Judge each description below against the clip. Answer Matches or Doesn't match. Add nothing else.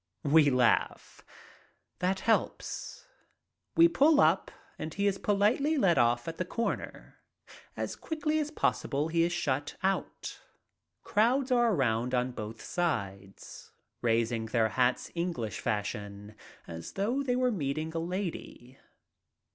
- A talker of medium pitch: Matches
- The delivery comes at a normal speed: Doesn't match